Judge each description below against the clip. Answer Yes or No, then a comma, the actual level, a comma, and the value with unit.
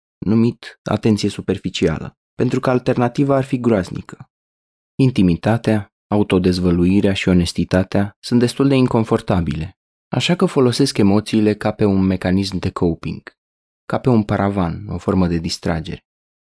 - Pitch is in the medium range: No, low, 105 Hz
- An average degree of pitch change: Yes, average, 4.5 semitones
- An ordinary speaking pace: Yes, average, 125 wpm